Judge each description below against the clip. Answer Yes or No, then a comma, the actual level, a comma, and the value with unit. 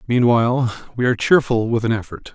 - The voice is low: Yes, low, 120 Hz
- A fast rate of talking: No, average, 180 wpm